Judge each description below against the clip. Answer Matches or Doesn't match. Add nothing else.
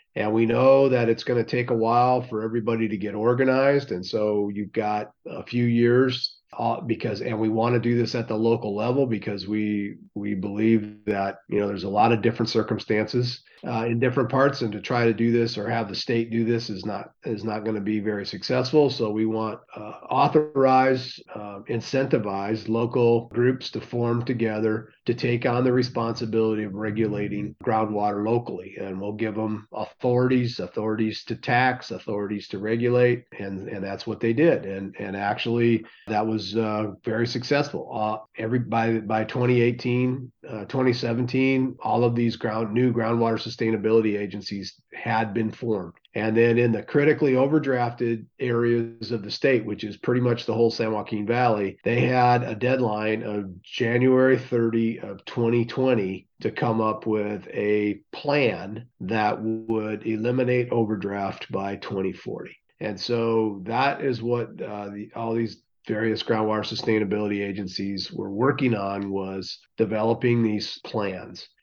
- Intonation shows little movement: Matches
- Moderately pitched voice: Doesn't match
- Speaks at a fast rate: Doesn't match